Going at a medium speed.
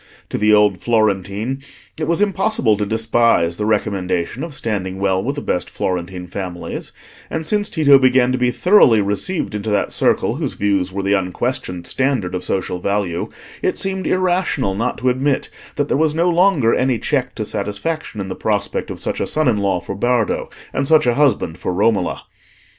Yes: average, 185 wpm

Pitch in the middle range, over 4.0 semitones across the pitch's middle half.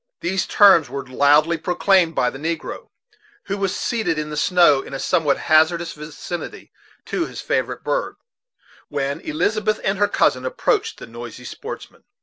Yes: medium, 170 Hz; average, 5.1 semitones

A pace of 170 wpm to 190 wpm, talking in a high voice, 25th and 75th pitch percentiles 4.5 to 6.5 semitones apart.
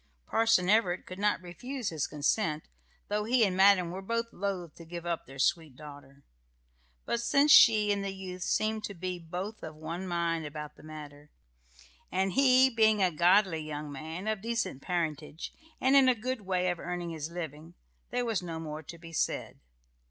No: average, 185 wpm; medium, 180 Hz; average, 4.9 semitones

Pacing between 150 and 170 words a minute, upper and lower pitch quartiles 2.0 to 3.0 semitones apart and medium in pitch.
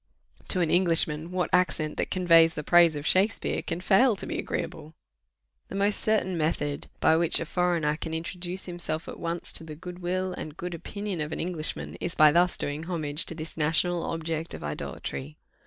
No: average, 190 wpm; narrow, 2.5 semitones; medium, 165 Hz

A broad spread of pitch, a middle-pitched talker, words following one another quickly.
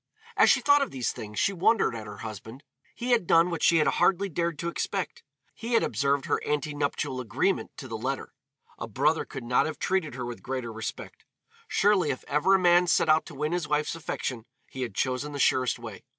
Yes: wide, 5.7 semitones; medium, 150 Hz; fast, 220 wpm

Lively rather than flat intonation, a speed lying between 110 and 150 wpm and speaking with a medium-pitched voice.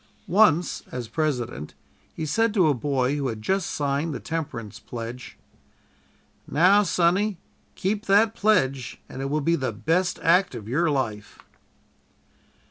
Yes: wide, 6.5 semitones; average, 140 wpm; medium, 150 Hz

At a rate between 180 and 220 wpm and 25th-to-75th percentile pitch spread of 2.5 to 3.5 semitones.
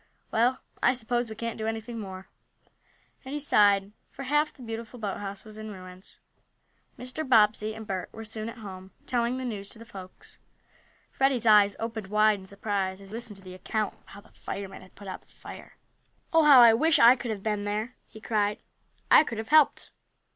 Yes: average, 200 wpm; average, 3.0 semitones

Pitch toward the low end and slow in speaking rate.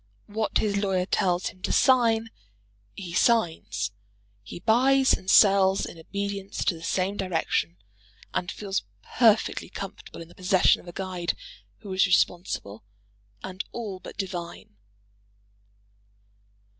No: high, 190 Hz; slow, 130 wpm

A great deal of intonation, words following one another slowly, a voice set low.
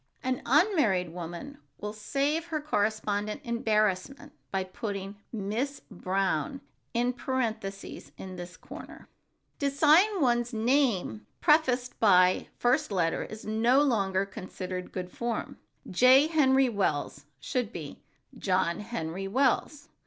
No: wide, 6.0 semitones; slow, 120 wpm; high, 220 Hz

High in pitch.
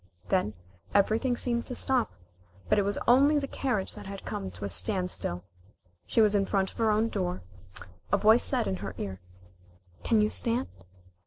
Yes: high, 205 Hz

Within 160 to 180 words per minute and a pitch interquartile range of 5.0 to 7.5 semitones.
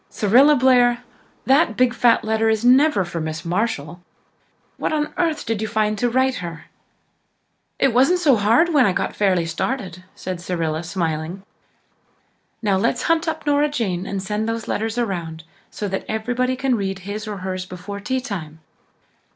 Yes: average, 165 wpm; wide, 5.6 semitones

